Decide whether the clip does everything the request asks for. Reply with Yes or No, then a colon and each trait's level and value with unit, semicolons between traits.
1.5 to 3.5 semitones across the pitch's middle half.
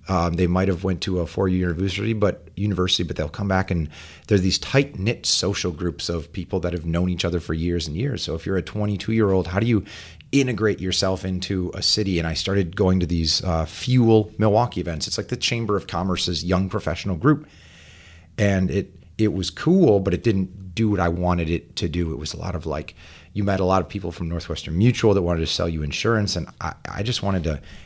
Yes: average, 3.2 semitones